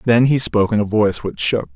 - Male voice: Yes, male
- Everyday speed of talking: No, fast, 275 wpm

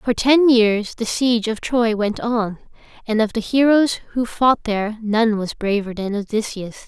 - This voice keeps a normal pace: Yes, average, 185 wpm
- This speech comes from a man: No, female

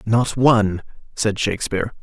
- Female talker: No, male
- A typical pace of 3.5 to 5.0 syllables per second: No, 5.2 syllables/s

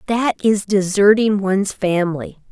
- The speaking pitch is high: Yes, high, 200 Hz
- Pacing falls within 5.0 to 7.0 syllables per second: No, 4.7 syllables/s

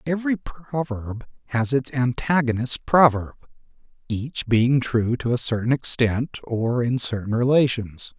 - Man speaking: Yes, male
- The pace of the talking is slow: Yes, slow, 125 wpm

